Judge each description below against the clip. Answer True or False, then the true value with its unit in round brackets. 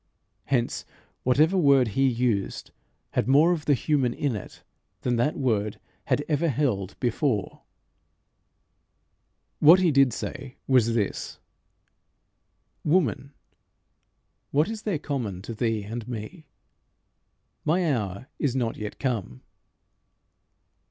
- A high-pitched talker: False (130 Hz)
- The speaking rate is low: True (115 wpm)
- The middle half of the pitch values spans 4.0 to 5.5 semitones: True (4.6 semitones)